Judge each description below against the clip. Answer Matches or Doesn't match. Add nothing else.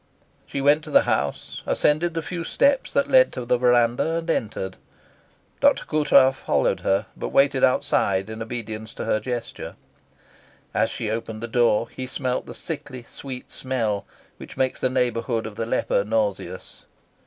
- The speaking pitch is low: Matches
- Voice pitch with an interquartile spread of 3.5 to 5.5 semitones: Matches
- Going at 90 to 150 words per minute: Doesn't match